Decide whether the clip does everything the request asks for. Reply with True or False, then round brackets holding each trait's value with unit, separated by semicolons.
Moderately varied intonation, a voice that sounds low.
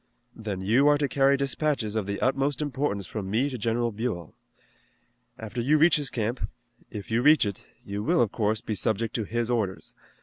True (4.7 semitones; 115 Hz)